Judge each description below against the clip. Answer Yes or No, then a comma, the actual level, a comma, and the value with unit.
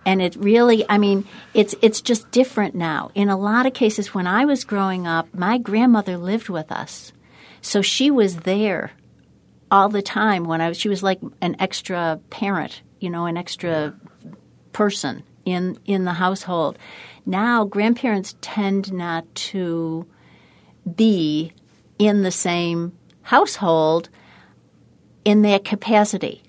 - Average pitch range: Yes, average, 3.5 semitones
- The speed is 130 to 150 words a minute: Yes, average, 145 wpm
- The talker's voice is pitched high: Yes, high, 195 Hz